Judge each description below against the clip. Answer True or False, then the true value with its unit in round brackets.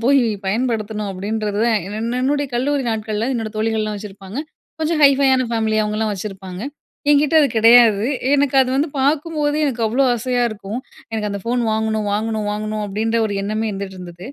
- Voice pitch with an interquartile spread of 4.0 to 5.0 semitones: False (3.5 semitones)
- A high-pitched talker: True (220 Hz)